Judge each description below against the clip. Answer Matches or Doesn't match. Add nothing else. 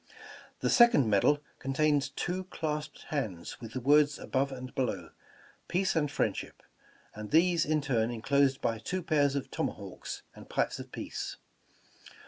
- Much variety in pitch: Doesn't match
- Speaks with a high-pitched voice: Doesn't match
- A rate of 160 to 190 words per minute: Doesn't match